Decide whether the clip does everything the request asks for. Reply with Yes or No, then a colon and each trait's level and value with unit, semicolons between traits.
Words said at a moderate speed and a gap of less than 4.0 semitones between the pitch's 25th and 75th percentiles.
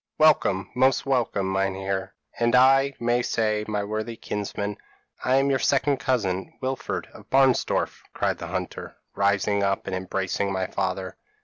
No: average, 145 wpm; average, 5.0 semitones